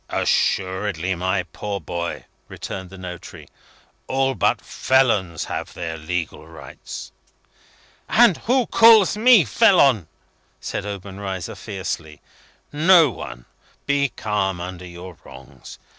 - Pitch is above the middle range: No, very low, 95 Hz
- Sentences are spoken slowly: Yes, slow, 110 wpm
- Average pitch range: No, wide, 7.4 semitones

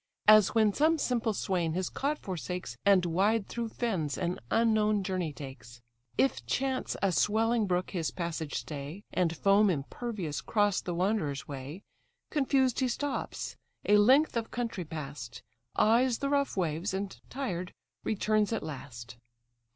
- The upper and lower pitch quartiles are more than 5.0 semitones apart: Yes, wide, 5.5 semitones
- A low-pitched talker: No, high, 195 Hz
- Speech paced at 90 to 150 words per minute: Yes, average, 145 wpm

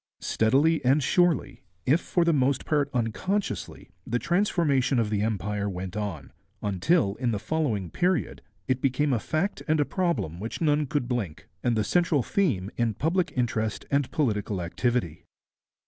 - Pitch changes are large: Yes, wide, 6.8 semitones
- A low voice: Yes, low, 125 Hz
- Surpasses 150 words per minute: Yes, average, 160 wpm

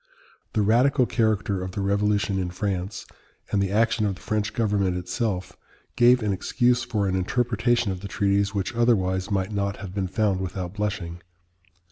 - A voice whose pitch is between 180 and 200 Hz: No, low, 100 Hz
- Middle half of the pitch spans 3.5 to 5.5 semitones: No, average, 2.8 semitones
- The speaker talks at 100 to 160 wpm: No, average, 170 wpm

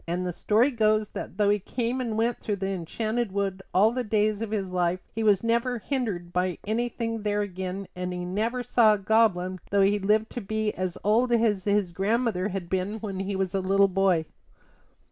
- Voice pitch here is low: No, high, 205 Hz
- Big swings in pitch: No, average, 3.0 semitones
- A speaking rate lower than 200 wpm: No, fast, 205 wpm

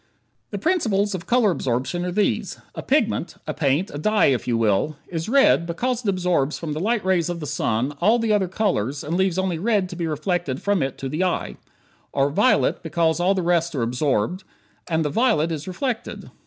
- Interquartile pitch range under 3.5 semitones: No, average, 5.1 semitones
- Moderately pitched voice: Yes, medium, 175 Hz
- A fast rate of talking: Yes, fast, 210 wpm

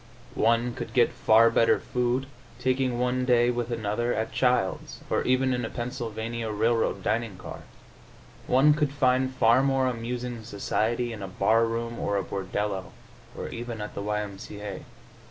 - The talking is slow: No, average, 170 wpm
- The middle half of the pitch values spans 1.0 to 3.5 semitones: Yes, narrow, 2.4 semitones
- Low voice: Yes, low, 115 Hz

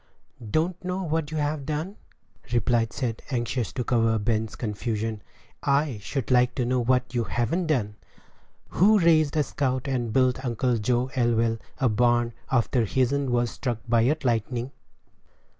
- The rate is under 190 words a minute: Yes, average, 145 wpm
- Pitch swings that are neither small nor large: Yes, average, 3.4 semitones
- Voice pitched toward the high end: No, low, 125 Hz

